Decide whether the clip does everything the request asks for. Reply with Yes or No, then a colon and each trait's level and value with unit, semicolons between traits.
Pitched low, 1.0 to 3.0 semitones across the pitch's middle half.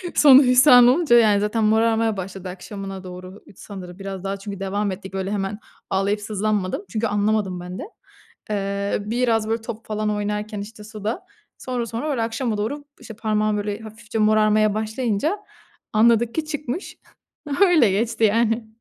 No: high, 215 Hz; narrow, 2.5 semitones